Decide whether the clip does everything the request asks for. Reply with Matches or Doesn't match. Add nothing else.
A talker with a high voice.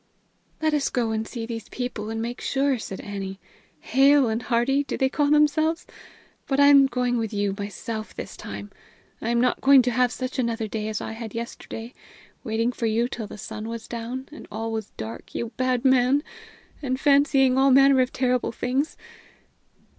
Matches